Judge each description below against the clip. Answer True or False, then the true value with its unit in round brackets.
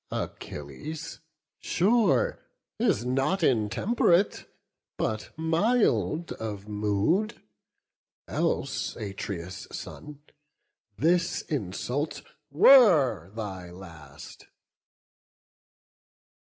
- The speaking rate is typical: False (60 wpm)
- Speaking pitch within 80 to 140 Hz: True (135 Hz)